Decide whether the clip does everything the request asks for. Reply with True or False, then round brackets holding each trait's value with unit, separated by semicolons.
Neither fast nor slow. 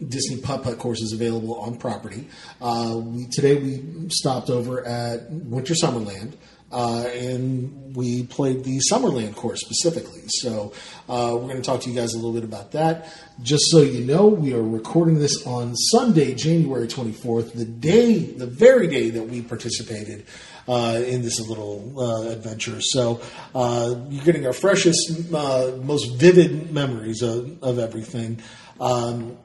True (160 wpm)